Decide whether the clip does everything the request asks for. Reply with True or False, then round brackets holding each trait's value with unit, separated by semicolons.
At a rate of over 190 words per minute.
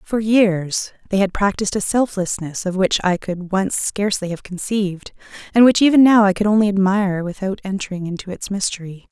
False (185 wpm)